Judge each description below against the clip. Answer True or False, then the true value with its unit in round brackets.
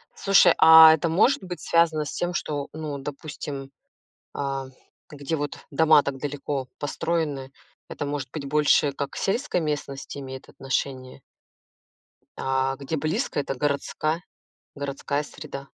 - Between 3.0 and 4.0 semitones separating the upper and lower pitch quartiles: False (2.4 semitones)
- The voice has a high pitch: False (145 Hz)